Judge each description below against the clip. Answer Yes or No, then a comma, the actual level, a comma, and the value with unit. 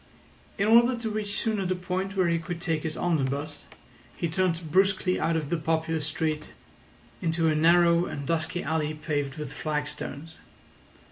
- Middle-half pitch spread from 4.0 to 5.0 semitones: No, average, 2.9 semitones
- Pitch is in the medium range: Yes, medium, 165 Hz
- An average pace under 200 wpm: Yes, average, 160 wpm